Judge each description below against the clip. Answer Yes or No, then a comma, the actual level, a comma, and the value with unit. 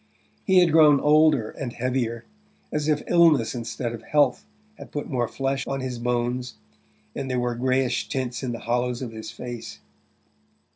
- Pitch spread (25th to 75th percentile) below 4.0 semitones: Yes, average, 3.1 semitones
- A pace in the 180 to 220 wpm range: No, average, 165 wpm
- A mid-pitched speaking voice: No, low, 125 Hz